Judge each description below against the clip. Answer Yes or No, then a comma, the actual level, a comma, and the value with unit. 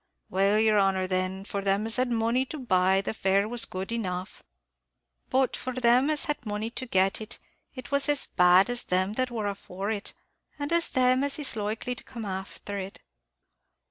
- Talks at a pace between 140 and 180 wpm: No, average, 190 wpm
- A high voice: Yes, high, 215 Hz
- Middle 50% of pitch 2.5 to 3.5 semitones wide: No, average, 4.6 semitones